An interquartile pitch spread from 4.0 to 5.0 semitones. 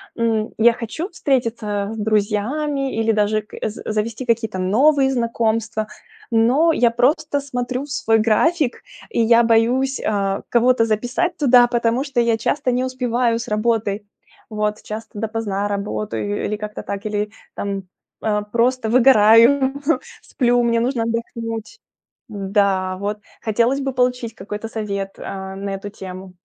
No: average, 3.0 semitones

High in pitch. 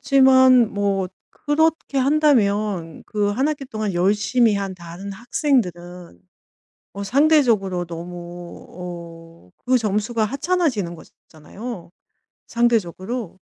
Yes: high, 205 Hz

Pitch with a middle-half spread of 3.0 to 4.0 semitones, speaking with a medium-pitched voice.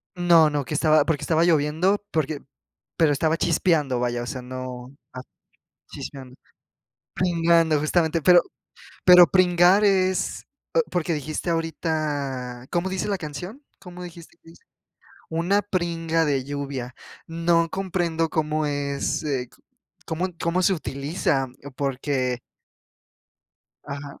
Yes: average, 3.6 semitones; medium, 160 Hz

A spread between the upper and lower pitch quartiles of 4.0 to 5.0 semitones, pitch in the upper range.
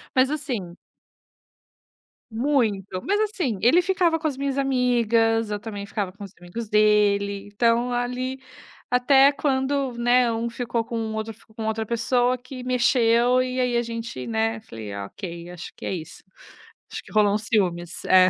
No: average, 3.5 semitones; high, 230 Hz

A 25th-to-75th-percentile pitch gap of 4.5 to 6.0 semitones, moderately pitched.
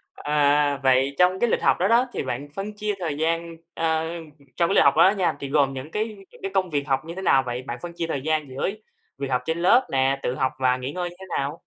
Yes: average, 4.8 semitones; medium, 150 Hz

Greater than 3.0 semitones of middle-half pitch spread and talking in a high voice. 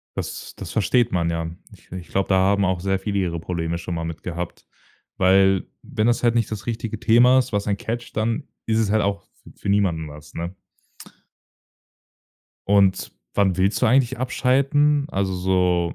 No: average, 4.1 semitones; low, 100 Hz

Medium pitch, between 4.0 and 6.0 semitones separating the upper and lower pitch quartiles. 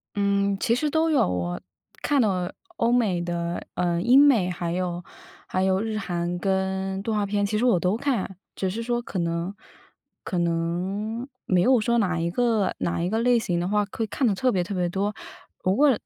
No: high, 195 Hz; average, 4.5 semitones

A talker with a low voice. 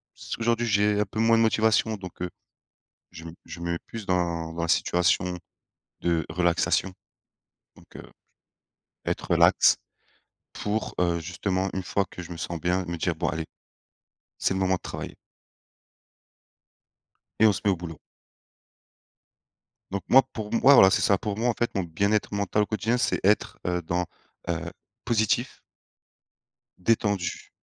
Yes: very low, 95 Hz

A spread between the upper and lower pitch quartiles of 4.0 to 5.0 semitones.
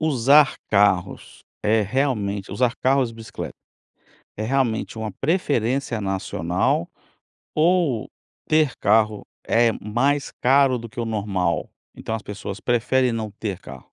Yes: average, 4.4 semitones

